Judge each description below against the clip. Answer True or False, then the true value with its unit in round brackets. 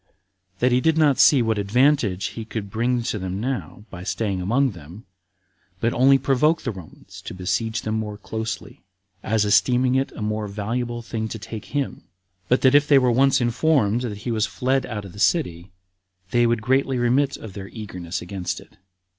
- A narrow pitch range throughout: False (4.0 semitones)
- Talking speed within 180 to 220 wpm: True (190 wpm)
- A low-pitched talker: True (115 Hz)